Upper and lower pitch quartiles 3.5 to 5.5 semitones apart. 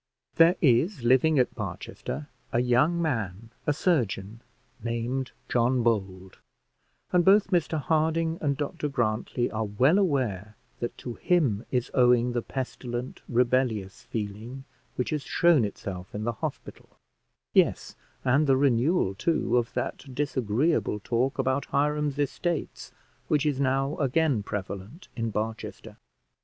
Yes: average, 4.6 semitones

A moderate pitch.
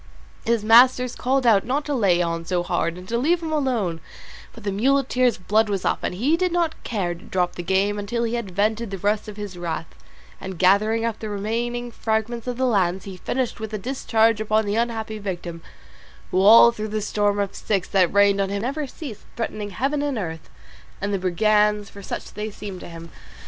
No: high, 215 Hz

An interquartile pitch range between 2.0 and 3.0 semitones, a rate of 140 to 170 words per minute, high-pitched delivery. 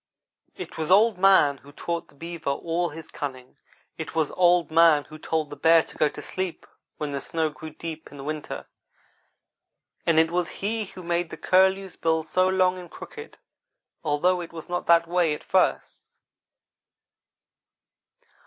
No: average, 2.7 semitones; average, 165 wpm; medium, 165 Hz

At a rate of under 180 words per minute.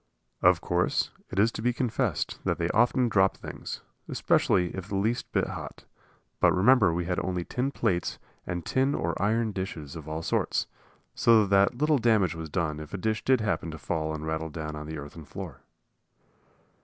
No: average, 190 wpm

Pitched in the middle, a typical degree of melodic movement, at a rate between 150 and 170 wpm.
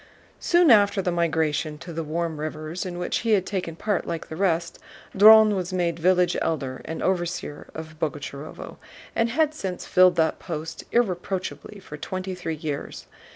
Yes: medium, 175 Hz; average, 3.2 semitones; average, 165 wpm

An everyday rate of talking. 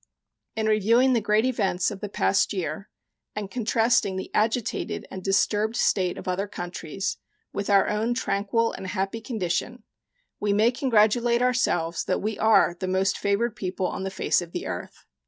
Yes: average, 170 wpm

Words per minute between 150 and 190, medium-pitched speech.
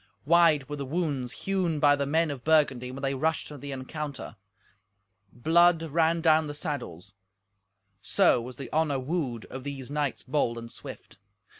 Yes: average, 165 wpm; medium, 145 Hz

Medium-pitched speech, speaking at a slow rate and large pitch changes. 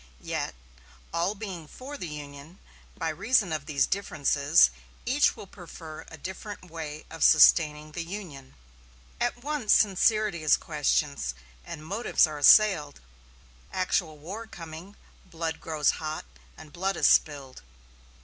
No: medium, 165 Hz; slow, 130 wpm; average, 4.7 semitones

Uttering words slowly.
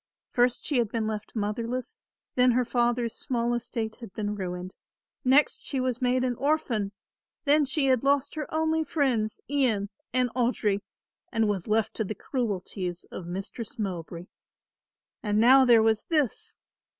No: average, 155 wpm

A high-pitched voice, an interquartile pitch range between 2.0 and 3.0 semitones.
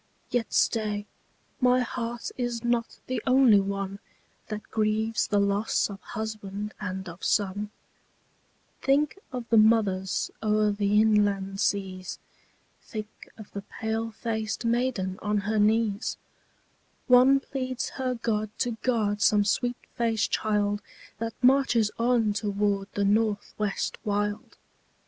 Yes: high, 215 Hz; narrow, 2.4 semitones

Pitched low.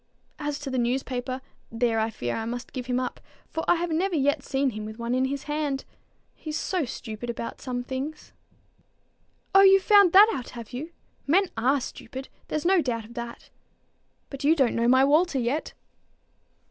No: very high, 265 Hz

